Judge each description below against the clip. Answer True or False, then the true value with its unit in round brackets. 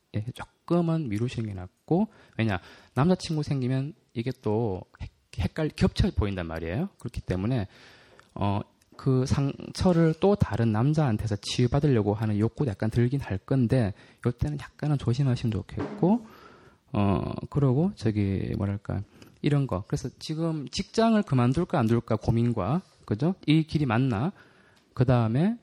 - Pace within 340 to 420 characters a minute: False (295 characters per minute)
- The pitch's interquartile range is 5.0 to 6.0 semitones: True (5.4 semitones)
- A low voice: True (125 Hz)